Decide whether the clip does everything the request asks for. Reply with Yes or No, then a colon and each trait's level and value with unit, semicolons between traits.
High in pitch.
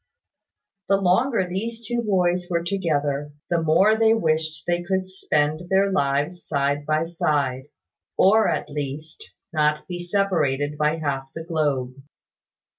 No: medium, 165 Hz